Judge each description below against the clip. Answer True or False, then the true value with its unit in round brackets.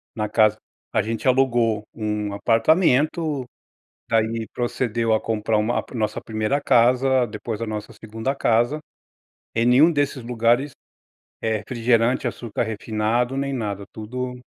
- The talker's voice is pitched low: True (115 Hz)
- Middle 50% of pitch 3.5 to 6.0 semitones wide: False (2.7 semitones)